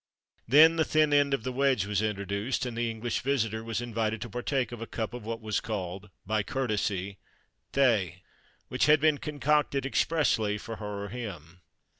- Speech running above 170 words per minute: Yes, average, 180 wpm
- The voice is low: Yes, low, 115 Hz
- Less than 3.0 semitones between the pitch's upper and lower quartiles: No, average, 4.7 semitones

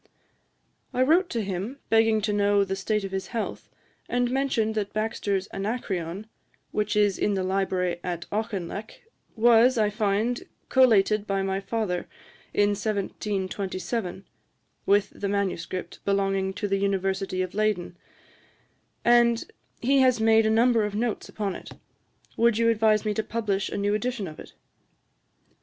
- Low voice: No, high, 210 Hz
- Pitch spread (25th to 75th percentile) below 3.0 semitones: Yes, narrow, 2.5 semitones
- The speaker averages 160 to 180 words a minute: No, average, 150 wpm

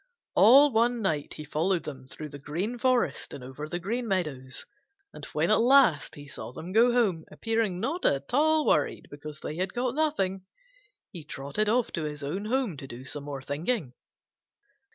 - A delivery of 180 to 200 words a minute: Yes, average, 185 wpm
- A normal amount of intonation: No, wide, 8.4 semitones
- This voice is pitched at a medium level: Yes, medium, 180 Hz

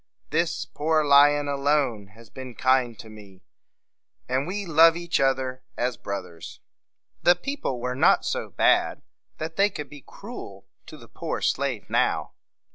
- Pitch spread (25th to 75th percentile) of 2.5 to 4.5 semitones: No, average, 5.0 semitones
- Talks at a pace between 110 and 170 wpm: Yes, average, 150 wpm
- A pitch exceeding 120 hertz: Yes, medium, 140 Hz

